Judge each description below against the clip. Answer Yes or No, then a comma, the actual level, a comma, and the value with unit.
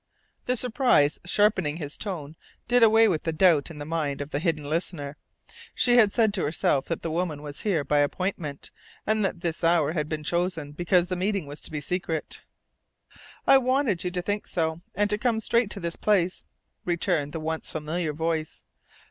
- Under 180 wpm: No, average, 190 wpm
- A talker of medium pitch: Yes, medium, 170 Hz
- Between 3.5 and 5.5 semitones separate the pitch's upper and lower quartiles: Yes, average, 4.7 semitones